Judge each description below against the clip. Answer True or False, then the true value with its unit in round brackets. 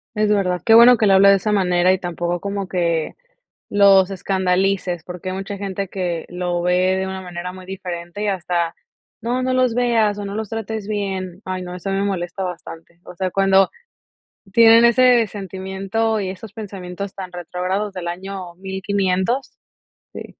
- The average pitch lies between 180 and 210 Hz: True (190 Hz)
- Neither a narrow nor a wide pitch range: False (2.2 semitones)